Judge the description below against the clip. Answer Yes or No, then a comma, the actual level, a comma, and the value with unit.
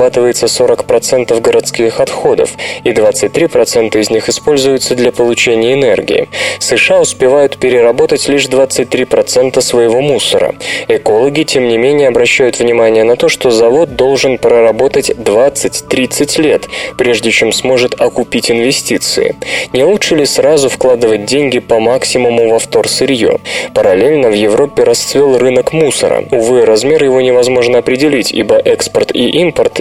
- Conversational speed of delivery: Yes, average, 125 wpm